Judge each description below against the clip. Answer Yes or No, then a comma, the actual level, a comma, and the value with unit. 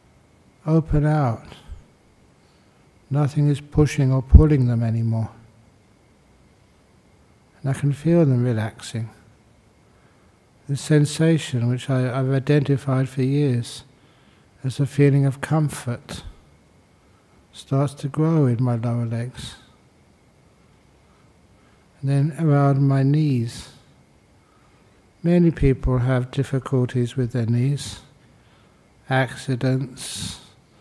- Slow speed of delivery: Yes, slow, 95 wpm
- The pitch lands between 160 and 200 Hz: No, low, 130 Hz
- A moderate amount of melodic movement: Yes, average, 3.3 semitones